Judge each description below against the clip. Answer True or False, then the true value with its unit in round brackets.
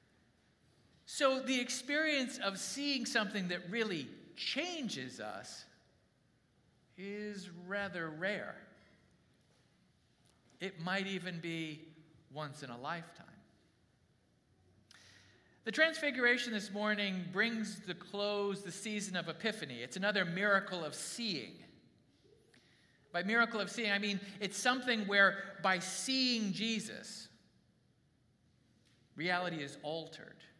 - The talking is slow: True (105 wpm)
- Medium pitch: False (195 Hz)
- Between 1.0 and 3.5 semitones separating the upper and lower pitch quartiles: False (5.0 semitones)